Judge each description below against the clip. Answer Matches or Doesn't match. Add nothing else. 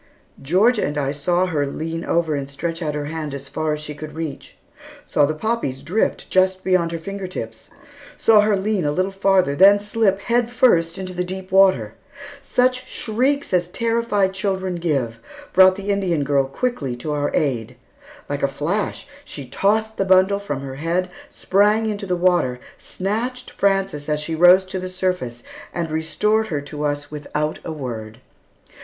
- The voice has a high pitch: Doesn't match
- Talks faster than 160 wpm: Matches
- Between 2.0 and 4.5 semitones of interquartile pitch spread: Doesn't match